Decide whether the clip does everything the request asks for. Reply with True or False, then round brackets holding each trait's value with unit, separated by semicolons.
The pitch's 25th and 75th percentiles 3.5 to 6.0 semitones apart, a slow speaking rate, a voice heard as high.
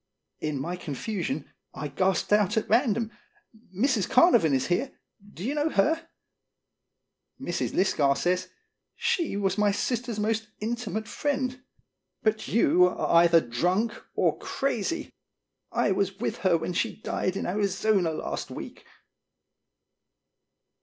True (4.6 semitones; 130 wpm; 205 Hz)